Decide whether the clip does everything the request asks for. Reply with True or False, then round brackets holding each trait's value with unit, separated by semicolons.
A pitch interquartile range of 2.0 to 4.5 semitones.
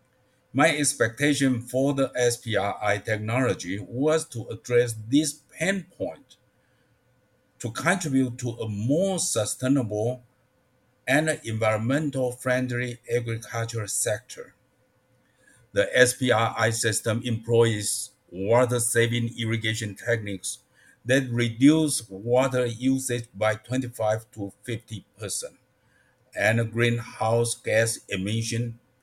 True (2.4 semitones)